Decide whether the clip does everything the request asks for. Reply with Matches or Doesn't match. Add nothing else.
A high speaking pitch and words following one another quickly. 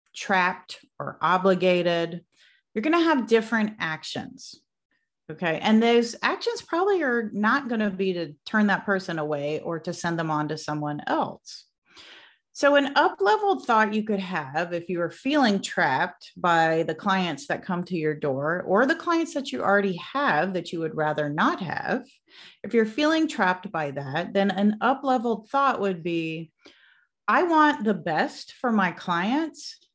Doesn't match